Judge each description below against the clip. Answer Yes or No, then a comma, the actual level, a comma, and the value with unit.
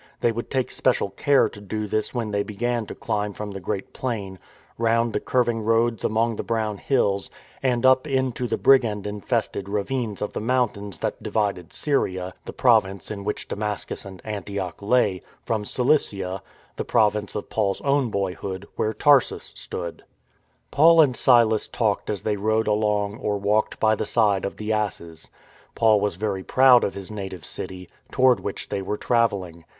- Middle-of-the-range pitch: No, low, 105 Hz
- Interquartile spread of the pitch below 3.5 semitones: Yes, average, 3.0 semitones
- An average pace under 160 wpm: No, average, 175 wpm